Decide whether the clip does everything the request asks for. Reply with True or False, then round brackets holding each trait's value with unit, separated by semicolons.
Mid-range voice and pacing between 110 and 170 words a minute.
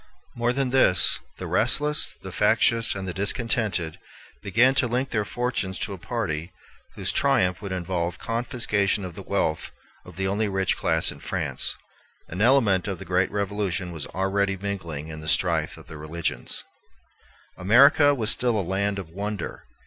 False (100 Hz; 165 wpm)